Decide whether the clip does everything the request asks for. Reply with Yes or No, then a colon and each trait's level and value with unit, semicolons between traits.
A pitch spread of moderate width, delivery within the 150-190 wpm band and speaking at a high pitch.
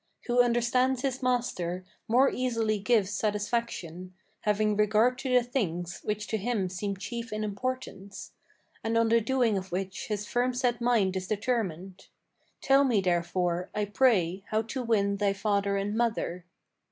Yes: average, 3.9 semitones; average, 155 wpm; high, 215 Hz